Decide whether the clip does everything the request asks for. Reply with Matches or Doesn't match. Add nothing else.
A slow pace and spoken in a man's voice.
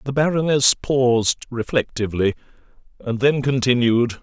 Matches